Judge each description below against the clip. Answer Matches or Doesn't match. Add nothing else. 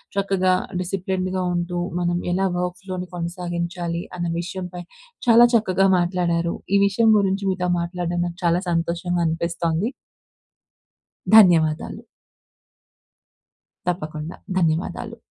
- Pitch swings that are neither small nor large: Doesn't match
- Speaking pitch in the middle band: Matches